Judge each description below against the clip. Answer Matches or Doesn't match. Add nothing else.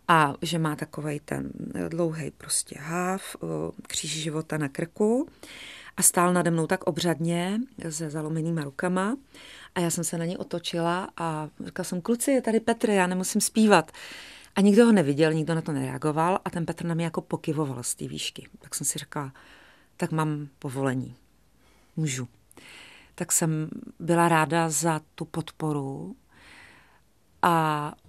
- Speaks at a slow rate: Doesn't match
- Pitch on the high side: Doesn't match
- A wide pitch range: Doesn't match